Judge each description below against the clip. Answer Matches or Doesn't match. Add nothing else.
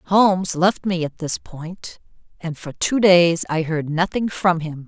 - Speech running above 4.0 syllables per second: Doesn't match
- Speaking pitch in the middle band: Matches